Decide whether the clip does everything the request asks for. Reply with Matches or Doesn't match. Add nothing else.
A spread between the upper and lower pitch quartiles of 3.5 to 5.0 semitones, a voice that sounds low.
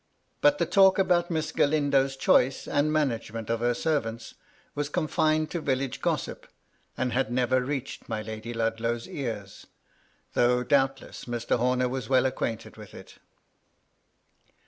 Matches